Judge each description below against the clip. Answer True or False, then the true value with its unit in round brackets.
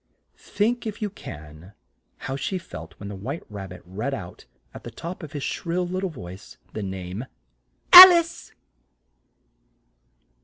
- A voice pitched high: False (135 Hz)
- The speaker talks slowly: False (155 wpm)